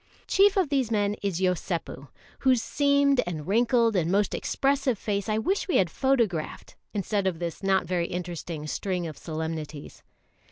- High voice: Yes, high, 200 Hz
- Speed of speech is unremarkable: Yes, average, 160 wpm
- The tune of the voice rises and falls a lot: Yes, wide, 6.5 semitones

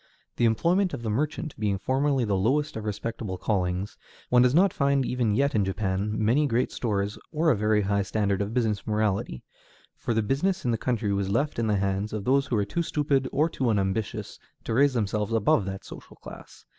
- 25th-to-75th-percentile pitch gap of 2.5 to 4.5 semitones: No, average, 4.9 semitones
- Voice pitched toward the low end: Yes, low, 110 Hz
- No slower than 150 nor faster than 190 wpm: No, fast, 205 wpm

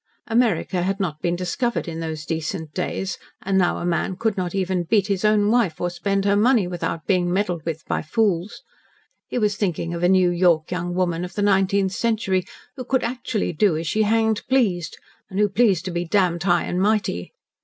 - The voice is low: No, medium, 185 Hz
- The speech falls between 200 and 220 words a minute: Yes, fast, 205 wpm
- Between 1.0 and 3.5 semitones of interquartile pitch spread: Yes, average, 3.1 semitones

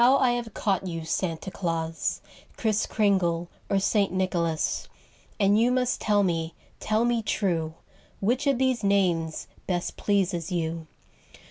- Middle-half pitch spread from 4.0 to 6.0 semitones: Yes, average, 4.5 semitones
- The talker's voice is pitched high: Yes, high, 195 Hz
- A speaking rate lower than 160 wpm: Yes, slow, 135 wpm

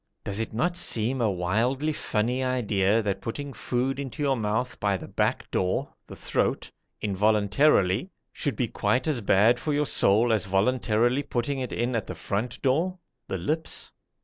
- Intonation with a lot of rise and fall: No, average, 4.4 semitones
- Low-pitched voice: Yes, low, 120 Hz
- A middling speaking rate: Yes, average, 170 wpm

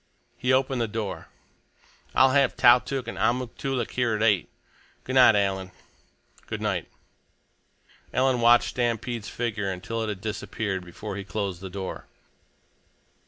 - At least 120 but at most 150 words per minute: Yes, average, 140 wpm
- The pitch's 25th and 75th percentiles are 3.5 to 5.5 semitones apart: Yes, average, 3.9 semitones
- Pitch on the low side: Yes, low, 115 Hz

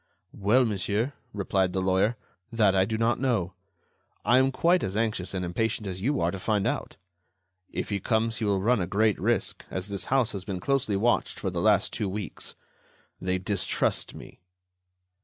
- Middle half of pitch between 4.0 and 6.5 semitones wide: No, average, 3.5 semitones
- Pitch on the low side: Yes, low, 105 Hz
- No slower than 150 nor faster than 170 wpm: No, average, 190 wpm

